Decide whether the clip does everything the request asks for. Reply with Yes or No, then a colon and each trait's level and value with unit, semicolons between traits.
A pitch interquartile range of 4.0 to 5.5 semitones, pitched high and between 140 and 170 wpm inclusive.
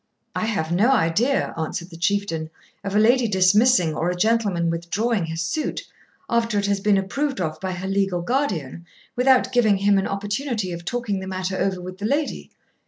No: average, 4.6 semitones; high, 195 Hz; average, 185 wpm